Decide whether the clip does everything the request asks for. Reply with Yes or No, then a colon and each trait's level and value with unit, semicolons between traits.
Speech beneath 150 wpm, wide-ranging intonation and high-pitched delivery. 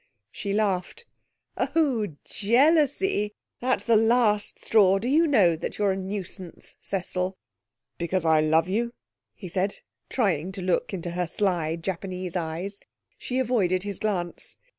No: average, 140 wpm; average, 3.9 semitones; high, 195 Hz